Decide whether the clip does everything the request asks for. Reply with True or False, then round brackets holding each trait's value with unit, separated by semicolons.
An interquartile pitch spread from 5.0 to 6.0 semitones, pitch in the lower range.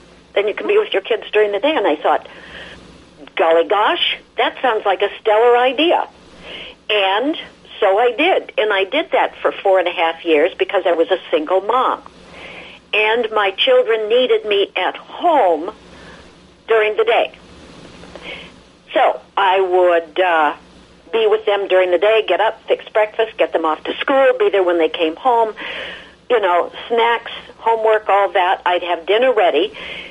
False (5.5 semitones; 215 Hz)